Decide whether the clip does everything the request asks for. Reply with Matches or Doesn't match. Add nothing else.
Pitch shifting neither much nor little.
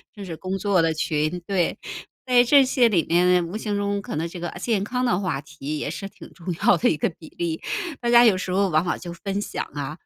Matches